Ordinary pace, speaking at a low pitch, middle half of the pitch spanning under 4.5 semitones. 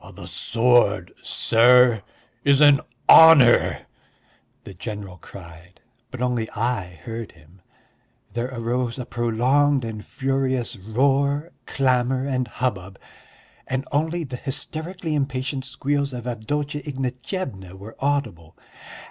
No: slow, 110 wpm; low, 125 Hz; average, 3.7 semitones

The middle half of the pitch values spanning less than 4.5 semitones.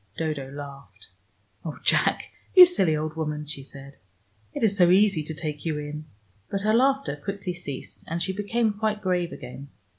No: wide, 5.4 semitones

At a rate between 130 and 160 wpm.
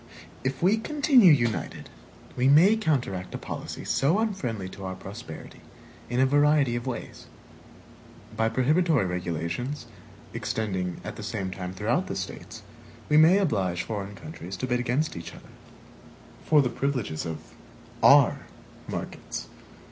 Yes: average, 140 wpm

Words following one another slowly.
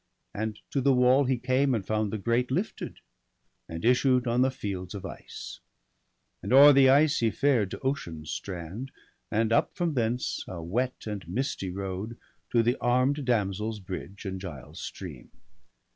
No: average, 165 wpm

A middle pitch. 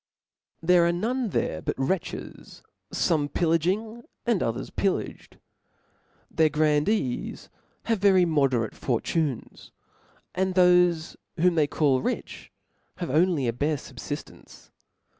Yes: medium, 165 Hz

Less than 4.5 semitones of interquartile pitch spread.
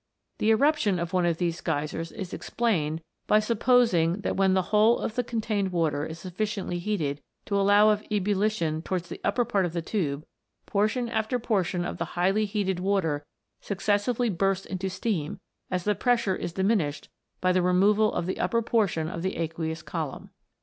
Yes: average, 3.9 semitones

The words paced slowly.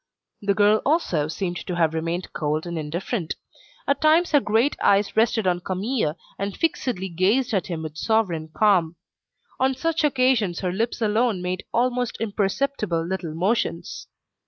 No: average, 155 wpm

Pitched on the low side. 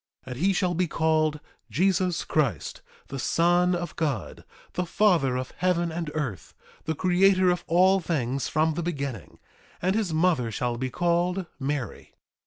No: medium, 165 Hz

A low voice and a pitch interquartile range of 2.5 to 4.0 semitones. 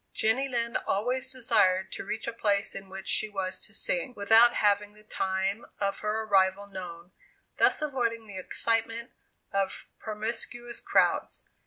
No: high, 215 Hz; average, 3.0 semitones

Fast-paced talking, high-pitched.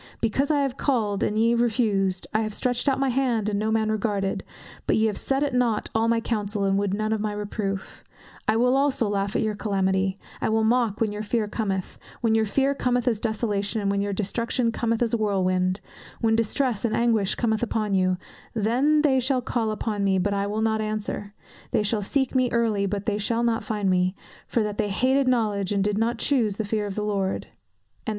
Yes: fast, 215 wpm; high, 215 Hz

